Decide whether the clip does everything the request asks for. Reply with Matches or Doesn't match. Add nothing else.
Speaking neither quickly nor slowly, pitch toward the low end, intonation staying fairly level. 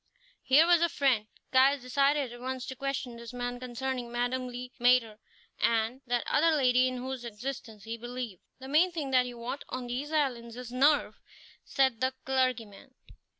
Doesn't match